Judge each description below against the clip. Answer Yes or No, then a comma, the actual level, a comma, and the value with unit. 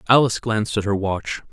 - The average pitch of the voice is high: No, low, 105 Hz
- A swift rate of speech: No, average, 195 wpm